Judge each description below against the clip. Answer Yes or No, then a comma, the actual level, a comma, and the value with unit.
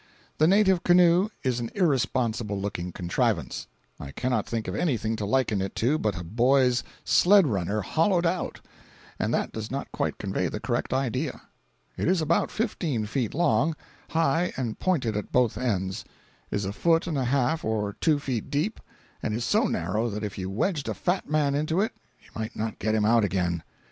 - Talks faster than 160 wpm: Yes, average, 185 wpm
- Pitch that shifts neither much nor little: No, wide, 6.9 semitones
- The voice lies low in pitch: Yes, low, 125 Hz